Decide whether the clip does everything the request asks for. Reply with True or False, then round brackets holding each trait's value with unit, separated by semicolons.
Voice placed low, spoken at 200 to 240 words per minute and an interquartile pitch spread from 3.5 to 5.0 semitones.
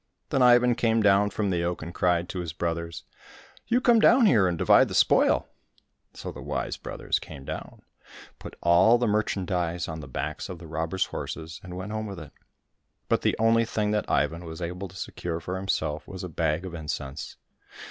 True (90 Hz; 205 wpm; 4.2 semitones)